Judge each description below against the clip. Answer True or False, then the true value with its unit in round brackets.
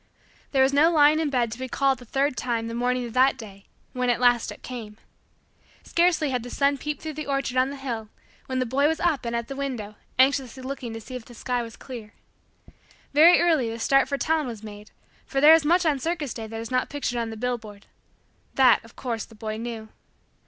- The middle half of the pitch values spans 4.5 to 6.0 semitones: False (3.4 semitones)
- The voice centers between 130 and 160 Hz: False (255 Hz)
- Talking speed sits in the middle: False (230 wpm)